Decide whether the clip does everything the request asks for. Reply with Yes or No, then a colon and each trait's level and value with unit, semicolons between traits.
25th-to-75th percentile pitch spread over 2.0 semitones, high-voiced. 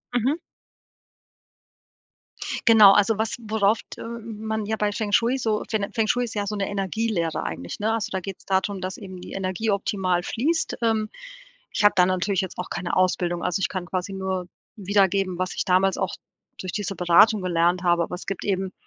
Yes: average, 2.8 semitones; high, 195 Hz